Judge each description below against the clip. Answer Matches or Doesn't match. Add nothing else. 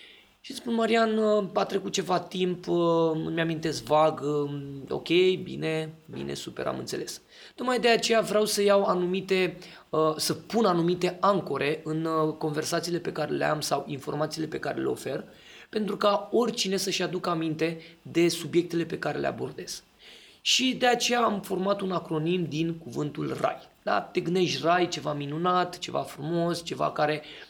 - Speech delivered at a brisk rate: Doesn't match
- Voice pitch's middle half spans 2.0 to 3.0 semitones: Doesn't match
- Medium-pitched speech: Matches